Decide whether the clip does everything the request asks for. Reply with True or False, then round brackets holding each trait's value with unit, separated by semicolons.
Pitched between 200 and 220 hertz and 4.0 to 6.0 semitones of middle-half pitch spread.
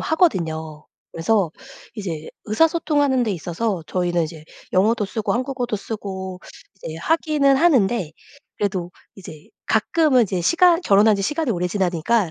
False (205 Hz; 6.8 semitones)